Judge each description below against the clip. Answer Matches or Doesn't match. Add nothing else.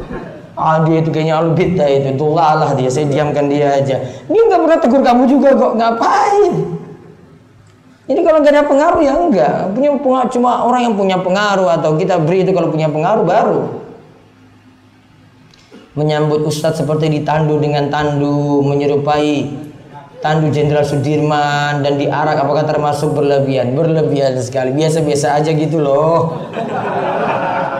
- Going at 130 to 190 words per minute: Matches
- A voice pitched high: Doesn't match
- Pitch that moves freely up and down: Doesn't match